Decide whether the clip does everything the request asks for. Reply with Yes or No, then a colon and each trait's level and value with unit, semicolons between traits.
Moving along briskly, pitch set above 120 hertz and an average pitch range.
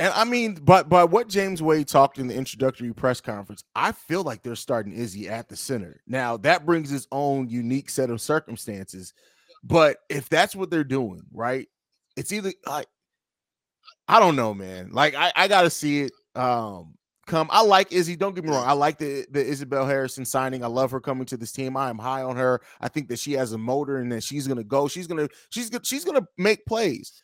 No: fast, 220 wpm; low, 135 Hz; wide, 5.8 semitones